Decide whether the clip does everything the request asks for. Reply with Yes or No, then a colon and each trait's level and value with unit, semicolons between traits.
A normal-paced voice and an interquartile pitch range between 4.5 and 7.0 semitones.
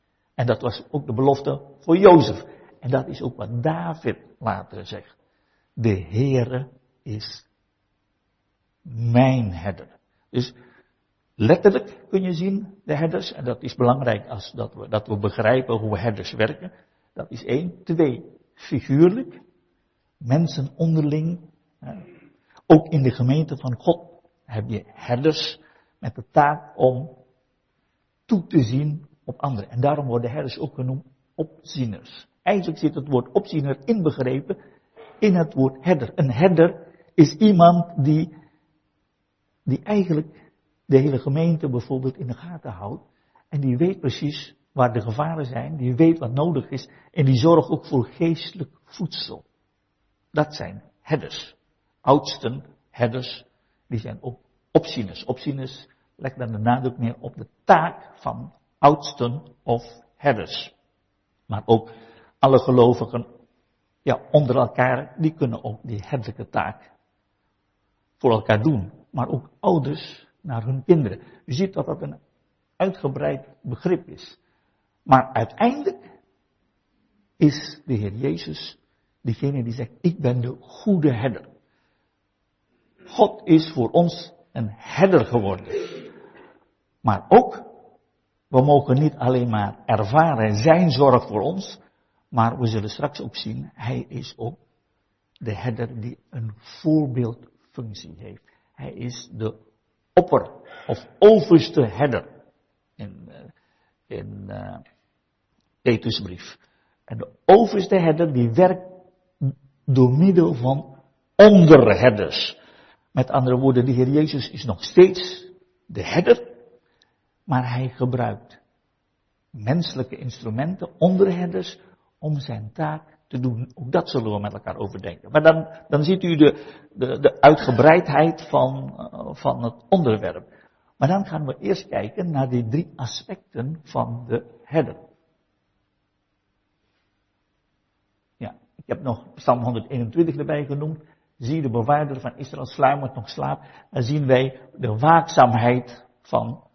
Yes: average, 130 wpm; average, 5.0 semitones